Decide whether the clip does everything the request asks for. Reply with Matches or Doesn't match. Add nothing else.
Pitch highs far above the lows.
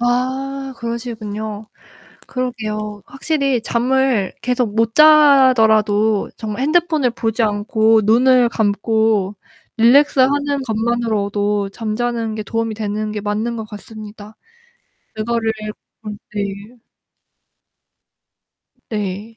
Doesn't match